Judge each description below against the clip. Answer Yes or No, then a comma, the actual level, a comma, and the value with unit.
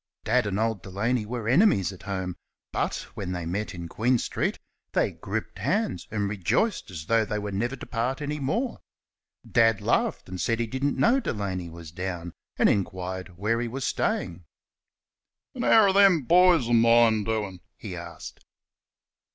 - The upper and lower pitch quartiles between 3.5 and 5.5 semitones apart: Yes, average, 5.1 semitones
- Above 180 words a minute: No, average, 170 wpm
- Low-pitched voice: Yes, low, 110 Hz